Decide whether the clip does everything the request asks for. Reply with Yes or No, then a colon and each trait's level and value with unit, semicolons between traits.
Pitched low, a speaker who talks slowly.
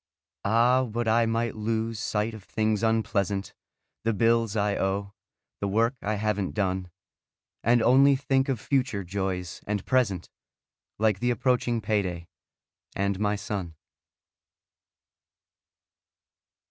Yes: low, 110 Hz; slow, 120 wpm